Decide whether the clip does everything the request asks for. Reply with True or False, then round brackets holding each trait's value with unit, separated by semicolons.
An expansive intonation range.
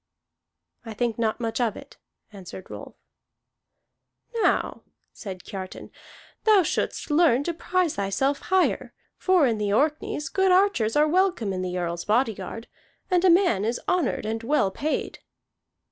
True (8.5 semitones)